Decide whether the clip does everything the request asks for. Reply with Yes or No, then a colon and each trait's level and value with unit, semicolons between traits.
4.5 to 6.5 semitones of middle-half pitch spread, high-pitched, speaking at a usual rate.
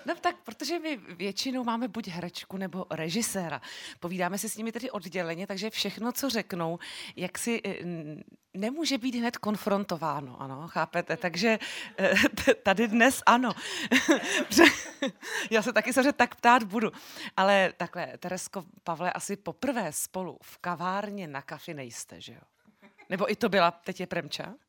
Yes: average, 5.2 semitones; high, 200 Hz; average, 150 wpm